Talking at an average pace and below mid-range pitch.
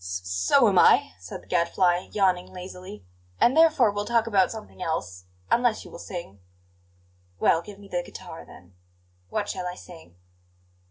No: average, 165 wpm; medium, 180 Hz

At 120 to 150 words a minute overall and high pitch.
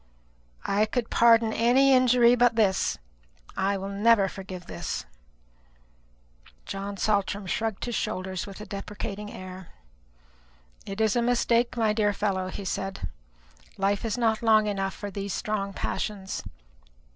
Yes: slow, 135 wpm; high, 205 Hz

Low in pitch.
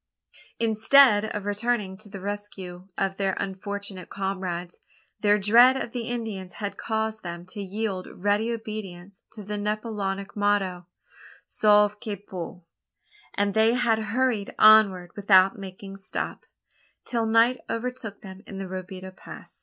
No: high, 205 Hz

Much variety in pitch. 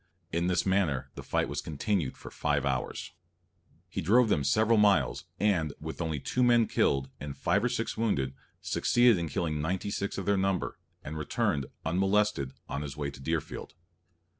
Yes: wide, 5.9 semitones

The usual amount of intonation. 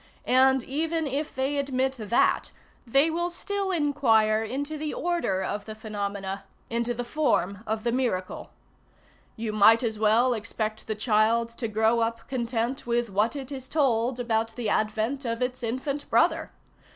Yes: average, 3.8 semitones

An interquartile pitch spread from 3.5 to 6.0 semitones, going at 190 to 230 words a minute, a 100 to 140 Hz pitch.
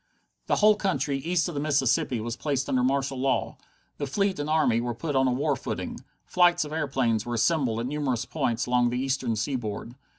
Yes: average, 3.8 semitones; average, 200 wpm; low, 135 Hz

